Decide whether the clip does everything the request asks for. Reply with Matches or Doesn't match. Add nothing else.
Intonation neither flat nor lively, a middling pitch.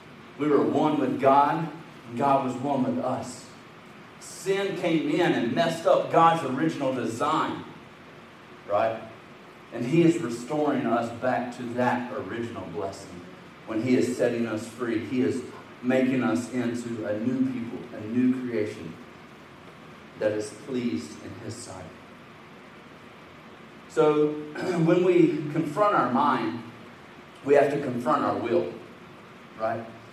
Doesn't match